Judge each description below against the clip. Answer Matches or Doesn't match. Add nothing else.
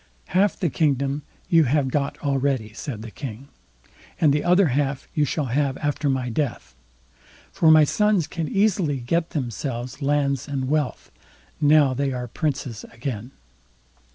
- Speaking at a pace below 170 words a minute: Matches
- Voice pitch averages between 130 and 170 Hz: Matches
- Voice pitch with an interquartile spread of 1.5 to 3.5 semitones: Matches